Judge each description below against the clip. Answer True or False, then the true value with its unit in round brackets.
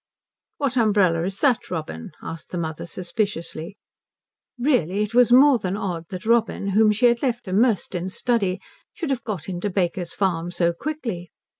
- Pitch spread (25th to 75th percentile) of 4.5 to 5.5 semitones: True (5.2 semitones)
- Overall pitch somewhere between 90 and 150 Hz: False (195 Hz)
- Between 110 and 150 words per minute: False (165 wpm)